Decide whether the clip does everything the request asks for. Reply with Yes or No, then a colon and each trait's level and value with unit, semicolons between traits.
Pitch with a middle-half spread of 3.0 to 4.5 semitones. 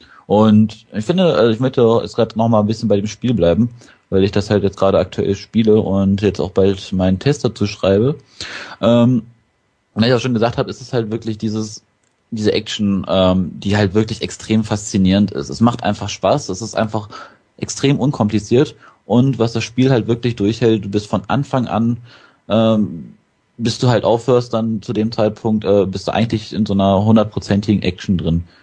No: narrow, 2.6 semitones